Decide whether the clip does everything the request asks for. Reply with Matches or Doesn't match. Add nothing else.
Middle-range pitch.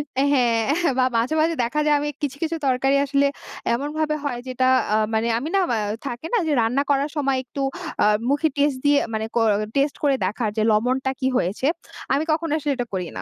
Doesn't match